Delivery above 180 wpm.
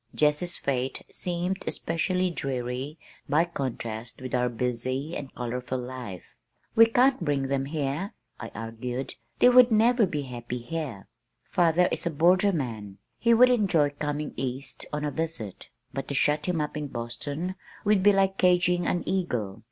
No: average, 155 wpm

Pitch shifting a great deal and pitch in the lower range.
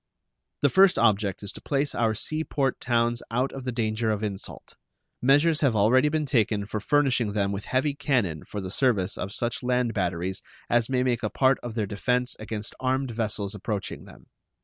No: average, 4.0 semitones; low, 115 Hz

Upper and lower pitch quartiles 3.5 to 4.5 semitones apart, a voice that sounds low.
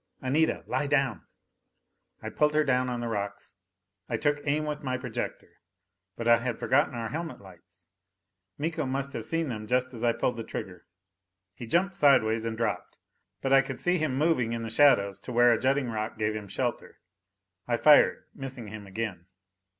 Yes: average, 4.2 semitones; low, 125 Hz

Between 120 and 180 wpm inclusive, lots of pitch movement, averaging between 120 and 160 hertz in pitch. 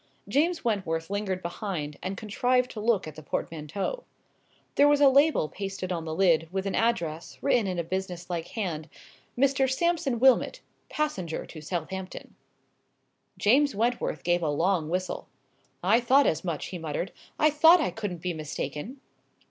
No: average, 160 wpm; wide, 7.0 semitones; high, 190 Hz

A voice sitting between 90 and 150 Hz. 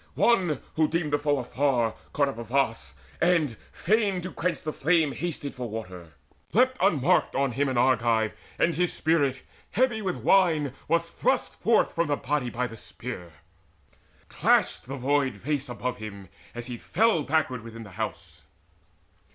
Yes: medium, 140 Hz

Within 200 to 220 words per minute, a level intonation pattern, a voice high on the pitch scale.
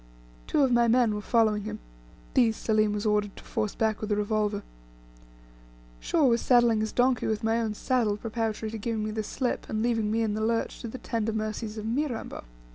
Yes: fast, 205 wpm; narrow, 1.6 semitones; high, 220 Hz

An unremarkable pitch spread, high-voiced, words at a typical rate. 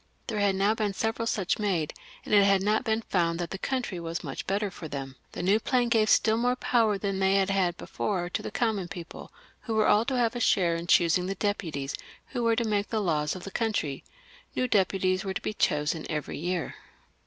No: average, 4.0 semitones; high, 195 Hz; fast, 235 wpm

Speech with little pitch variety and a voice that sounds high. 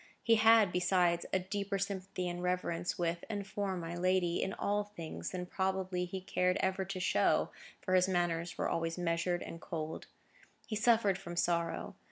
No: narrow, 1.9 semitones; medium, 180 Hz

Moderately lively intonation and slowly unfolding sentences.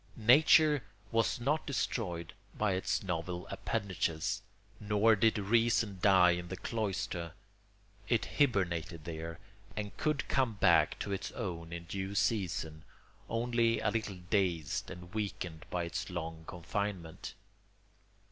Yes: average, 4.7 semitones; slow, 125 wpm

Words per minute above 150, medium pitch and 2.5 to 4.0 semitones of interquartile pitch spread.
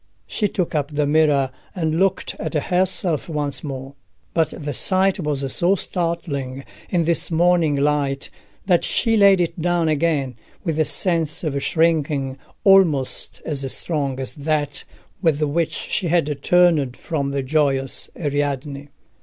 No: average, 145 wpm; medium, 155 Hz; average, 3.5 semitones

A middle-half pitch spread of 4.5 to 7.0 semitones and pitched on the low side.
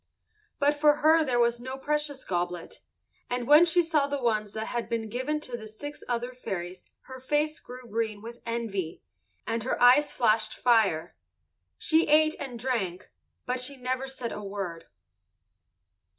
No: average, 5.0 semitones; high, 245 Hz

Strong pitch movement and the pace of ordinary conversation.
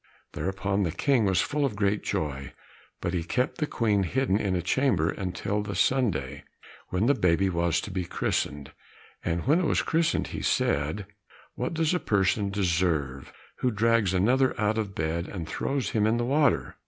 Yes: wide, 5.7 semitones; average, 180 wpm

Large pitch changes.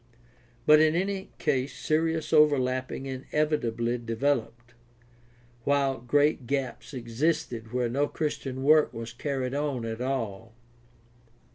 No: average, 4.1 semitones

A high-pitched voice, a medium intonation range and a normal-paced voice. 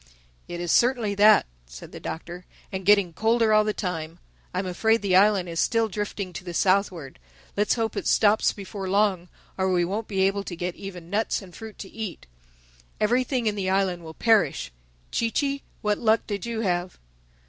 Yes: high, 195 Hz; average, 3.5 semitones; average, 180 wpm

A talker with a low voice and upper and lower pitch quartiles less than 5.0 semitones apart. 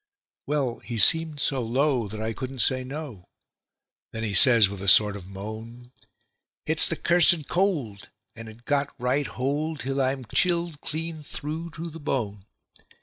No: low, 130 Hz; wide, 5.4 semitones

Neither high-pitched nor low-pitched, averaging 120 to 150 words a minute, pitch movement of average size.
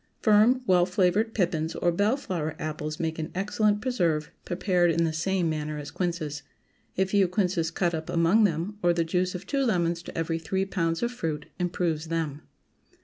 No: medium, 175 Hz; average, 185 wpm; average, 3.1 semitones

